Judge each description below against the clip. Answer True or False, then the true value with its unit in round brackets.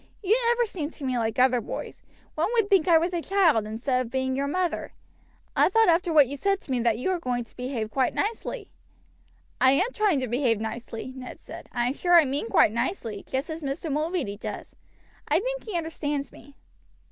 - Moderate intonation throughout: False (6.3 semitones)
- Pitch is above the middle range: True (285 Hz)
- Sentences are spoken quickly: True (210 wpm)